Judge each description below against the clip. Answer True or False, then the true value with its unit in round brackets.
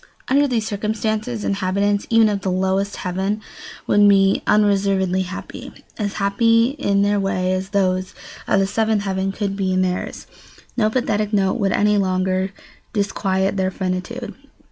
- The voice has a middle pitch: False (200 Hz)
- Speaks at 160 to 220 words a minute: False (150 wpm)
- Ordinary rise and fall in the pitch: False (1.8 semitones)